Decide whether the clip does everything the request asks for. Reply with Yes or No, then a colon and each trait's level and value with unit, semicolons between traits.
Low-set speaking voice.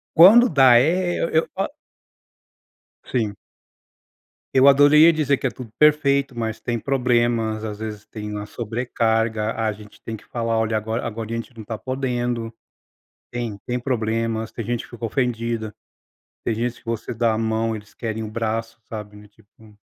Yes: low, 115 Hz